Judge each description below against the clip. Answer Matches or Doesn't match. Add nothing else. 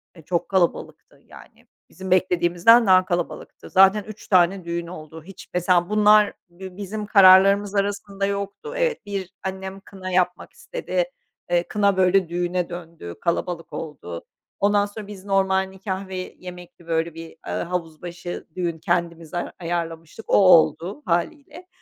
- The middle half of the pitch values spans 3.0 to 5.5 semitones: Doesn't match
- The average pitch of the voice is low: Doesn't match